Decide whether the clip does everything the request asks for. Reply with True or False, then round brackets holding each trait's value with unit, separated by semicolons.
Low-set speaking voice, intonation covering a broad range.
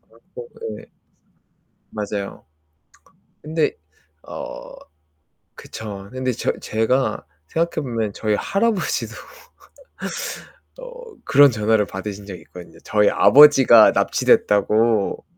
True (110 Hz; 6.4 semitones)